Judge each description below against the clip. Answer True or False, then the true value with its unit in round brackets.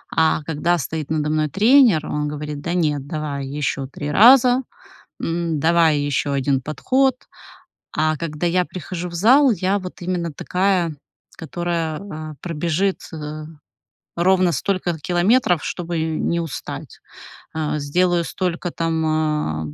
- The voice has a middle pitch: True (165 Hz)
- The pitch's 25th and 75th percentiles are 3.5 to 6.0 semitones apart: False (3.1 semitones)